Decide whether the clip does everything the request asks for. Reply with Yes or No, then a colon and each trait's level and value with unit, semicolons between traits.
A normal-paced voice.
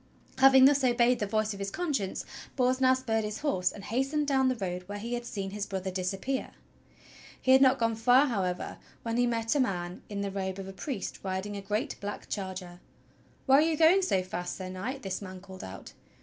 No: fast, 220 wpm